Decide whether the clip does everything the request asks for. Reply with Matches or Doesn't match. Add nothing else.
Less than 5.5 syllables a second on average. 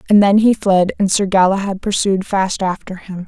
Matches